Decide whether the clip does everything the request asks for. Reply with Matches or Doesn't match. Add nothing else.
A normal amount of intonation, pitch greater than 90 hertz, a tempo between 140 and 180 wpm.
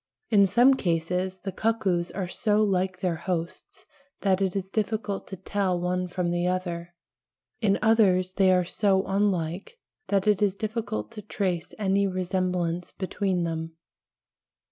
Doesn't match